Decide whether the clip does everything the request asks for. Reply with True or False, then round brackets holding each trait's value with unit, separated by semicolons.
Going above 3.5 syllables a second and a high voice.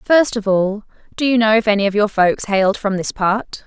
True (5.3 syllables/s; 210 Hz)